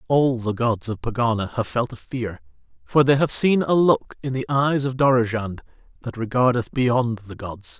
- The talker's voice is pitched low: Yes, low, 120 Hz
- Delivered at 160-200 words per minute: Yes, average, 190 wpm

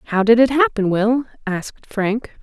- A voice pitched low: No, high, 225 Hz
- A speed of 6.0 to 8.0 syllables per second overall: No, 4.6 syllables/s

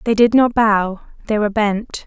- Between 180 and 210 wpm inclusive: Yes, fast, 205 wpm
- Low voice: No, high, 215 Hz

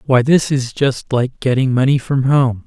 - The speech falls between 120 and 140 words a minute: No, average, 200 wpm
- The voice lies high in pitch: No, low, 130 Hz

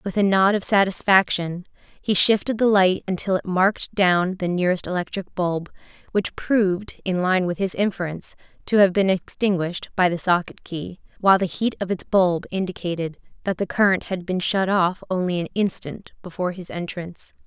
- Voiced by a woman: Yes, female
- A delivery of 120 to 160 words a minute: No, average, 180 wpm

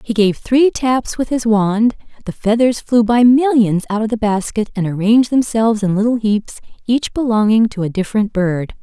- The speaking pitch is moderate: No, high, 220 Hz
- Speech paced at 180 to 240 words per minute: Yes, average, 185 wpm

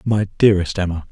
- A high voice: No, very low, 95 Hz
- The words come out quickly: No, average, 160 wpm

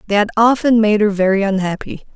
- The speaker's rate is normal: Yes, average, 195 wpm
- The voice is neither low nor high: No, high, 210 Hz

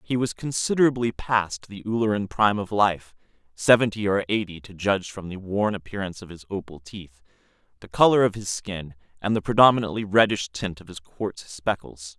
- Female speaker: No, male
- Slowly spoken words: No, average, 170 wpm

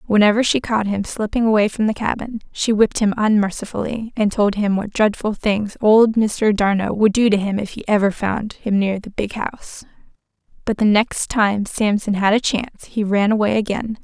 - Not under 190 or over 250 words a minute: Yes, average, 200 wpm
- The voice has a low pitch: No, high, 210 Hz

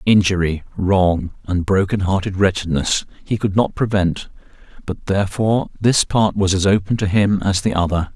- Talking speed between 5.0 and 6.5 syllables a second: No, 4.8 syllables/s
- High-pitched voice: No, very low, 95 Hz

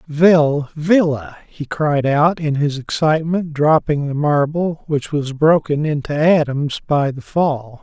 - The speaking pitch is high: No, medium, 150 Hz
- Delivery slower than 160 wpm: Yes, average, 140 wpm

